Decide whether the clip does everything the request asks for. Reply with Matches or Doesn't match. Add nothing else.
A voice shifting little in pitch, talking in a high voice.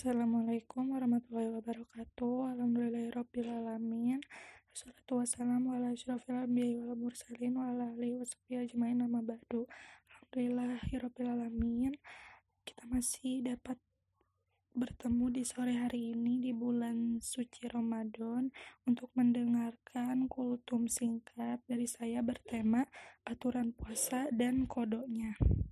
Matches